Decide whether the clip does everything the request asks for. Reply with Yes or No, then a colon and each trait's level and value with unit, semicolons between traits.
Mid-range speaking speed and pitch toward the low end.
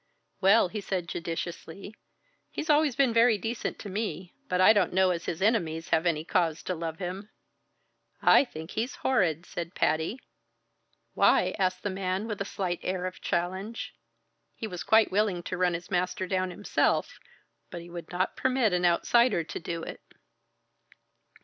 No: average, 170 wpm; medium, 185 Hz